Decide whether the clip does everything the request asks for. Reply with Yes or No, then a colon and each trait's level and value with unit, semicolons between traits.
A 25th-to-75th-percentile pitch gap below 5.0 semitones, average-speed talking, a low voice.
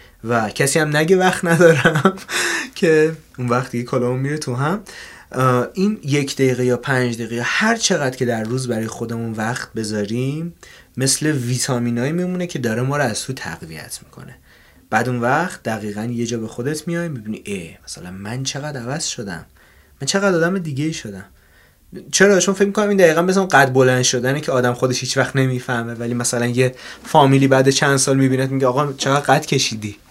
No: average, 4.3 semitones; fast, 175 wpm; low, 130 Hz